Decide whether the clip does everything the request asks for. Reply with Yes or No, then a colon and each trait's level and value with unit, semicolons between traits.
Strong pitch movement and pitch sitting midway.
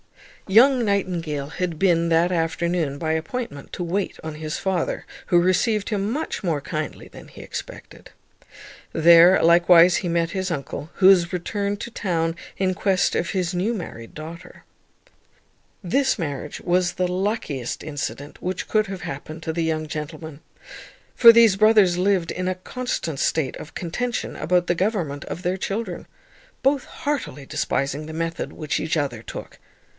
No: average, 3.6 semitones; medium, 175 Hz